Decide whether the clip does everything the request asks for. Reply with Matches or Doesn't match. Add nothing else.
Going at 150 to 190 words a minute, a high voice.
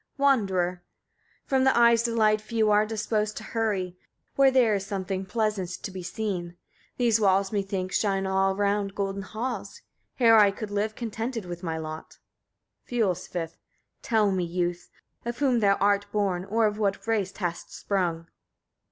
Matches